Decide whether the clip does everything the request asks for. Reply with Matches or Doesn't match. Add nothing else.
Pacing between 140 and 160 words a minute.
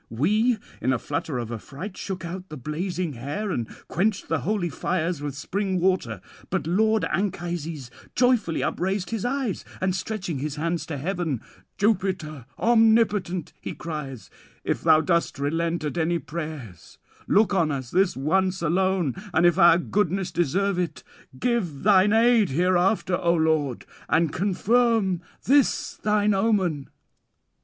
Matches